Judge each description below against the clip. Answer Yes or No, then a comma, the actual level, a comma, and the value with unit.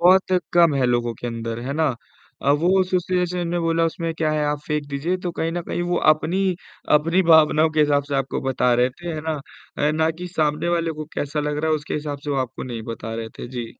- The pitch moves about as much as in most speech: Yes, average, 3.4 semitones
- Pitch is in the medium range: Yes, medium, 155 Hz